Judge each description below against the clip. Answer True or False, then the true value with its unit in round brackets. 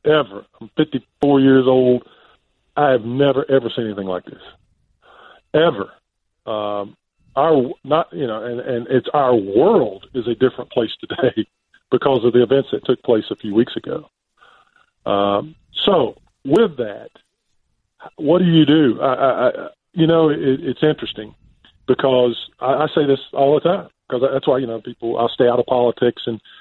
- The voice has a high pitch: False (125 Hz)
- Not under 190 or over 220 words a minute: False (175 wpm)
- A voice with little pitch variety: False (3.0 semitones)